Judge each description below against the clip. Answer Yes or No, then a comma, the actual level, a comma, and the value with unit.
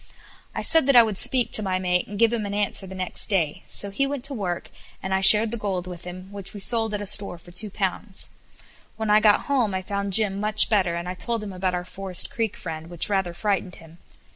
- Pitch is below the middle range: No, high, 195 Hz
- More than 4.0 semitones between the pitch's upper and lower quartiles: No, average, 2.9 semitones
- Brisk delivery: Yes, fast, 250 wpm